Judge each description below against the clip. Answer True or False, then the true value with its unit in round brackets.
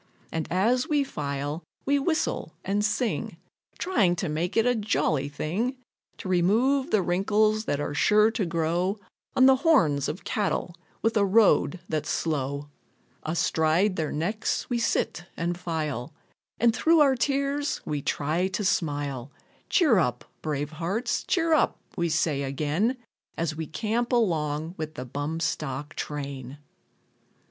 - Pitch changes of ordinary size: False (6.9 semitones)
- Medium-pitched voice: True (175 Hz)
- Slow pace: False (145 wpm)